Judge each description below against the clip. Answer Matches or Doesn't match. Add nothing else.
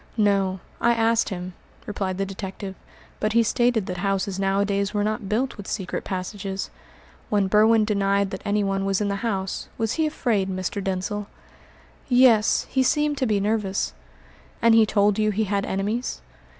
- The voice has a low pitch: Doesn't match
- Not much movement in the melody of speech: Matches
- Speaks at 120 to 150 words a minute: Doesn't match